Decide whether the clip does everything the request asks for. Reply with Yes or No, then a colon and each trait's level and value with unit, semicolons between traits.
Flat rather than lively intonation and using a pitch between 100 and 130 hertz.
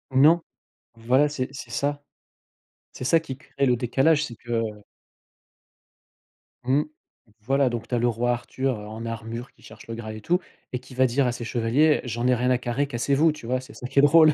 No: average, 3.2 semitones; low, 125 Hz